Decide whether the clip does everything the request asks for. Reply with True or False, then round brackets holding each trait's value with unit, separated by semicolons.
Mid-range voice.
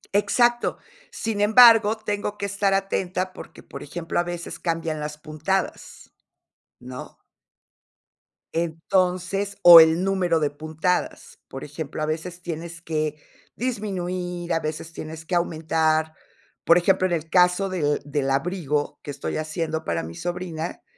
True (170 Hz)